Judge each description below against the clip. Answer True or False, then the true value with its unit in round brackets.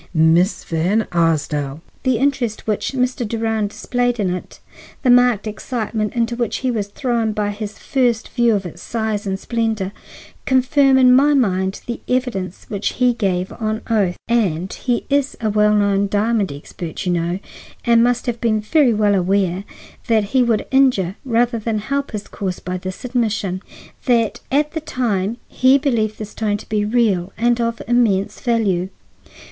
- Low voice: False (220 Hz)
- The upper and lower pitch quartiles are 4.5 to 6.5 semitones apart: False (3.7 semitones)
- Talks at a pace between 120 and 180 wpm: True (170 wpm)